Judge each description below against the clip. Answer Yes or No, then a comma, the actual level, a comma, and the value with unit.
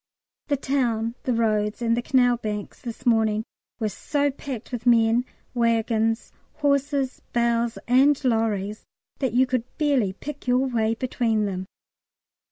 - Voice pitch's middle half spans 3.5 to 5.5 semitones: No, narrow, 2.6 semitones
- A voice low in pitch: No, high, 235 Hz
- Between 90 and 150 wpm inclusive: Yes, average, 140 wpm